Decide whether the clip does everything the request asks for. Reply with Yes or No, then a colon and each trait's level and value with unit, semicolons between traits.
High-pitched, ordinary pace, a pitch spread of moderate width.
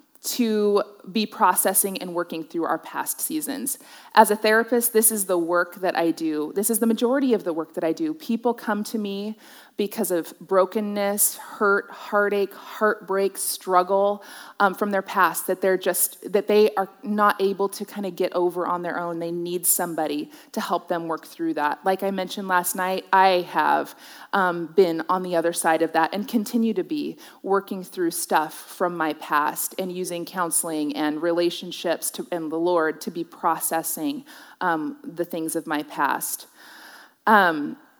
Yes: high, 195 Hz; average, 180 wpm; average, 4.0 semitones